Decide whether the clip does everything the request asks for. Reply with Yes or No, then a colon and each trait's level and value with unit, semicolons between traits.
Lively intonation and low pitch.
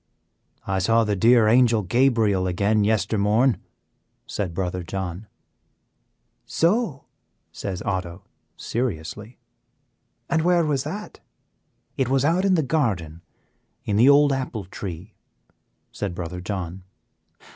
Yes: wide, 6.2 semitones; low, 110 Hz